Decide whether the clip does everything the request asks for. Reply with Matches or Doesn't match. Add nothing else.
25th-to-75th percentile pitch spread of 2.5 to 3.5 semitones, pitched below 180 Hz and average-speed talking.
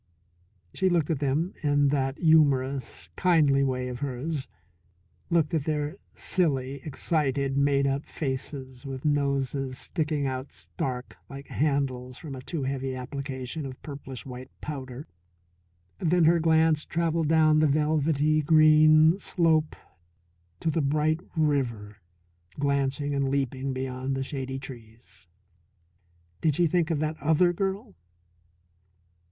Doesn't match